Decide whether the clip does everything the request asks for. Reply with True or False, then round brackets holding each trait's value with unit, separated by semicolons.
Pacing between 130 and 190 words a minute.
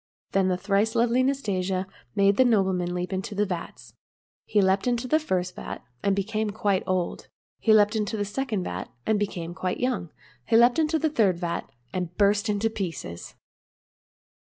True (175 wpm)